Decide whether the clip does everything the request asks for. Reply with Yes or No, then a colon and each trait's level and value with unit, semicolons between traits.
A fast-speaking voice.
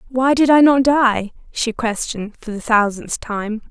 No: average, 180 wpm